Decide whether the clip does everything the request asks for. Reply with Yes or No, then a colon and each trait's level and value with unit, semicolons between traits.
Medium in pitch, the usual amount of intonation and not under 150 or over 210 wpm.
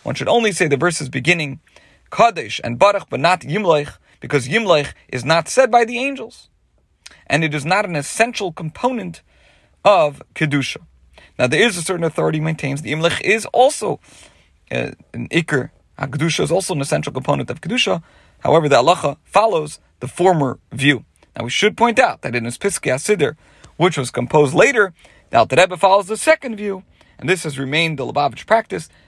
No: medium, 160 Hz; wide, 6.1 semitones; average, 175 wpm